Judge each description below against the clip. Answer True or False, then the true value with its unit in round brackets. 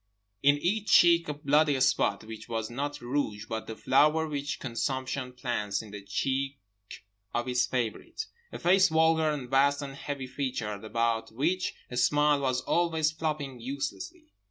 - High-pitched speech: False (135 Hz)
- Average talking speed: True (155 wpm)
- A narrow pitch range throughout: False (4.0 semitones)